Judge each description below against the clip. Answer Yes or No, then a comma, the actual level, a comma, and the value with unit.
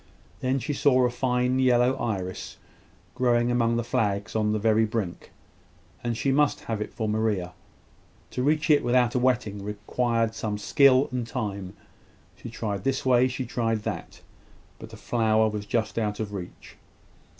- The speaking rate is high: No, average, 165 wpm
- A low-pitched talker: Yes, low, 115 Hz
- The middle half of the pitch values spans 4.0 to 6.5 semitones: No, average, 2.9 semitones